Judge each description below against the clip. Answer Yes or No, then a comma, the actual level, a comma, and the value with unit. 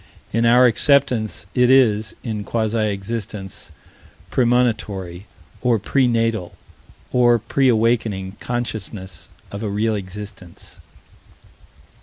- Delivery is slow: Yes, slow, 100 wpm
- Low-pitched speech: Yes, low, 110 Hz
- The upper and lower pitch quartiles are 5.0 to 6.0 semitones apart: No, average, 3.0 semitones